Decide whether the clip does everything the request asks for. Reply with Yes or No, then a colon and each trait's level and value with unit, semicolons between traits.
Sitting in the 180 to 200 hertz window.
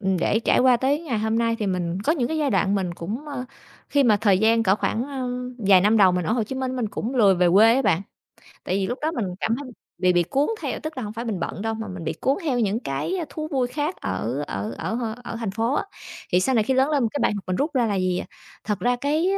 No: high, 225 Hz